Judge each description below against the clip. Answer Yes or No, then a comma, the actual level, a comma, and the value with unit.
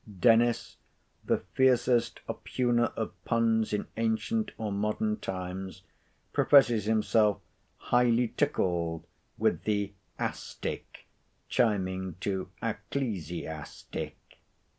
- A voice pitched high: No, low, 110 Hz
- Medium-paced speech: No, slow, 90 wpm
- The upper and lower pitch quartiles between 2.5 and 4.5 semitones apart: Yes, average, 3.8 semitones